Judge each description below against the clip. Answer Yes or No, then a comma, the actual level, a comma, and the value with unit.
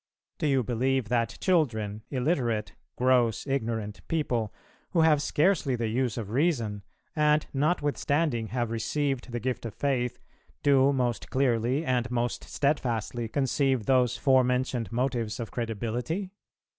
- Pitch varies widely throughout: No, average, 3.3 semitones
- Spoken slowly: Yes, slow, 130 wpm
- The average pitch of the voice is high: No, low, 125 Hz